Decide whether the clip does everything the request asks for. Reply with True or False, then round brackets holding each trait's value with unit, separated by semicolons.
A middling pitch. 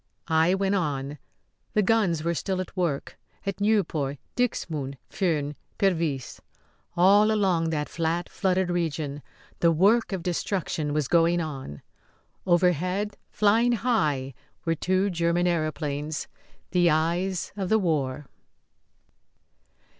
True (170 Hz)